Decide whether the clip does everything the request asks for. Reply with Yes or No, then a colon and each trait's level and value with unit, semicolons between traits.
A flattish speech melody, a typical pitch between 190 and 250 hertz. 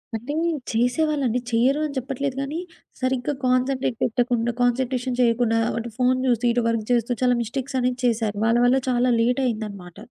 Yes: narrow, 2.0 semitones; high, 245 Hz